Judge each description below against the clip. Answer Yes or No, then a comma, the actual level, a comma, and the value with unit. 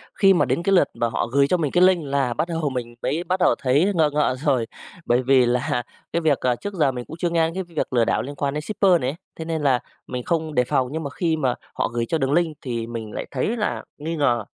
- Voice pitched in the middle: Yes, medium, 145 Hz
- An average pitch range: Yes, average, 4.8 semitones